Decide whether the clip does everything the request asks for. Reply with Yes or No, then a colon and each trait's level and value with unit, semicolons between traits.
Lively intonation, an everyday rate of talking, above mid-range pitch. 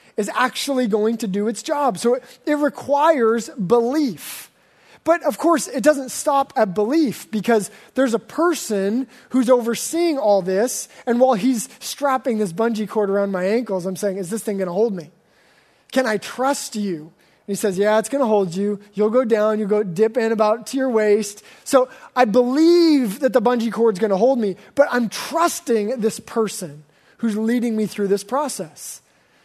No: average, 3.8 semitones; average, 185 wpm; high, 230 Hz